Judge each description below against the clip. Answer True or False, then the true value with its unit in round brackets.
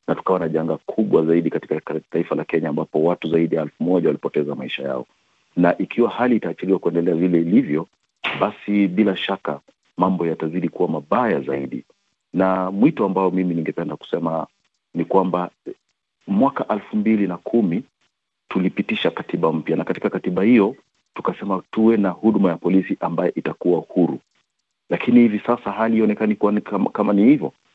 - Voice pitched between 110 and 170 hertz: False (95 Hz)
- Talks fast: True (150 wpm)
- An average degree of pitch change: True (3.7 semitones)